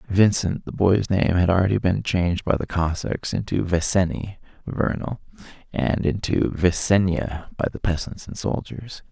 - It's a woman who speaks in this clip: No, male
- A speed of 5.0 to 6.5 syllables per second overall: No, 4.6 syllables/s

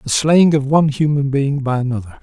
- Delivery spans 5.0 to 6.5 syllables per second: Yes, 5.5 syllables/s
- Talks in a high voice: No, medium, 140 Hz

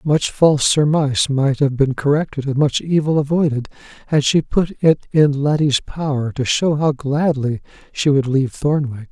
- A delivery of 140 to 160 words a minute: No, average, 170 wpm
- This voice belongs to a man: Yes, male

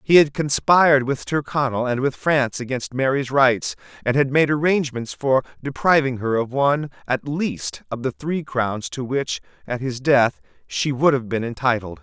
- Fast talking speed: No, average, 180 wpm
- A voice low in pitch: Yes, low, 130 Hz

